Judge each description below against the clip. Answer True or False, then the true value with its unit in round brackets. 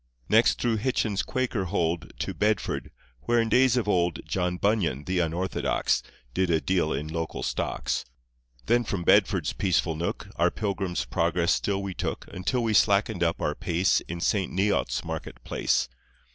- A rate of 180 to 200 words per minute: False (160 wpm)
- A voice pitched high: False (95 Hz)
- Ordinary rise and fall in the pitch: True (4.0 semitones)